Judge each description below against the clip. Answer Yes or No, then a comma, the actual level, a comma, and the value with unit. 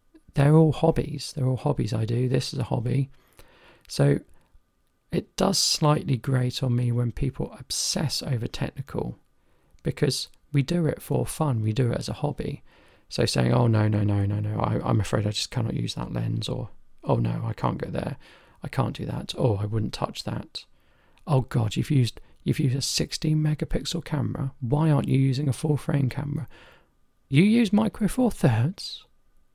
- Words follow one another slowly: No, average, 185 wpm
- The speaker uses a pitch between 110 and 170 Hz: Yes, low, 135 Hz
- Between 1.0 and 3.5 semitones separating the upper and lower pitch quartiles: No, average, 4.5 semitones